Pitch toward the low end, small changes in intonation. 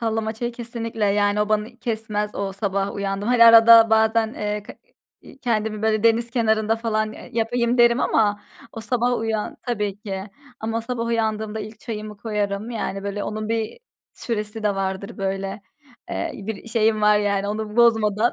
No: high, 220 Hz; narrow, 1.7 semitones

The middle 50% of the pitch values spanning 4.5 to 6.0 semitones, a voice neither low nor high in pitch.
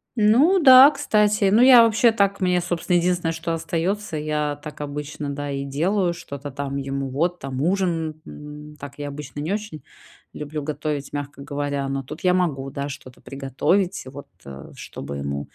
Yes: average, 4.8 semitones; medium, 150 Hz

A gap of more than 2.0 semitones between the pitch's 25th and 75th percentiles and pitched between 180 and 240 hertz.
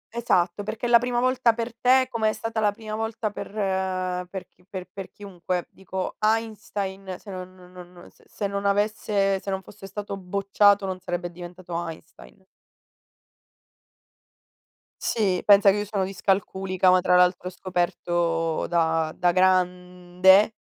Yes: narrow, 2.5 semitones; high, 190 Hz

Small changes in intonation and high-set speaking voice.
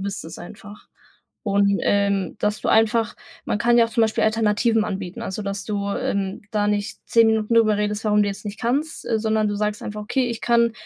Yes: narrow, 1.9 semitones; high, 210 Hz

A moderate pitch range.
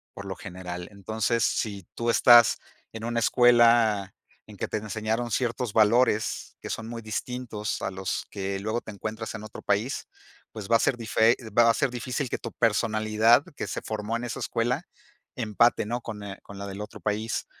No: narrow, 2.2 semitones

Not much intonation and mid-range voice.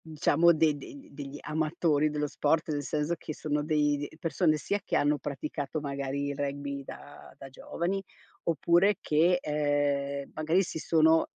Yes: narrow, 2.1 semitones; medium, 150 Hz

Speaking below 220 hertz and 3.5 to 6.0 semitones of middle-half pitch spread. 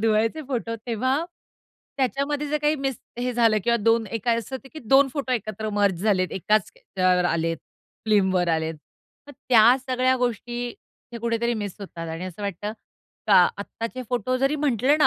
No: high, 230 Hz; average, 4.2 semitones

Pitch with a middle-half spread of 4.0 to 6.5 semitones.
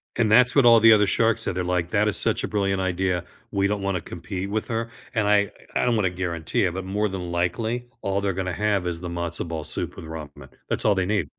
No: average, 3.3 semitones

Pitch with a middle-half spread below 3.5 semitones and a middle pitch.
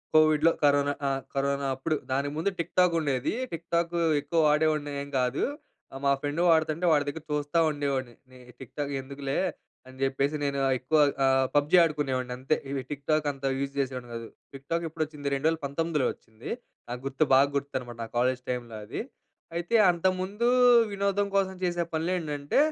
Yes: average, 3.1 semitones; medium, 145 Hz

